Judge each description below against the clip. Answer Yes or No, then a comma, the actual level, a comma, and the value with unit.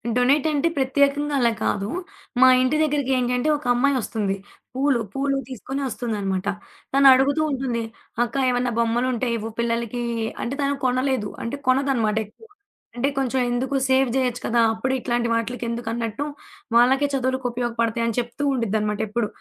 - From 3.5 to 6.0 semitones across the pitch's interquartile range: No, average, 2.7 semitones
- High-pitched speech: Yes, very high, 250 Hz